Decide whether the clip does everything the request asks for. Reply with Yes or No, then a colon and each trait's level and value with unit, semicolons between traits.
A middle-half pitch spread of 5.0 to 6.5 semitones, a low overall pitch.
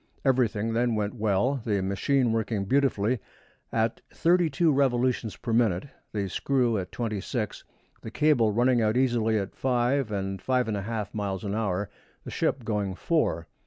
No: average, 3.8 semitones; low, 115 Hz